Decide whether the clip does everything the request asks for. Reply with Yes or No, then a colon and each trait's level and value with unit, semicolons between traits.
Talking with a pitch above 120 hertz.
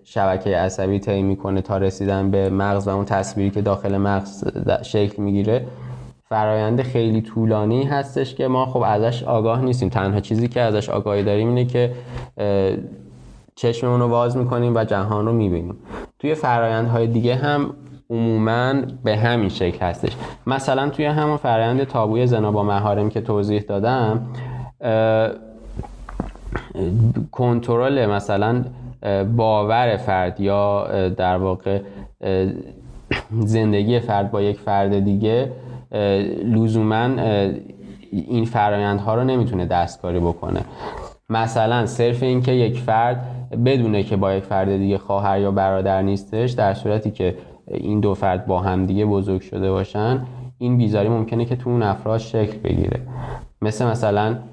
No: low, 110 Hz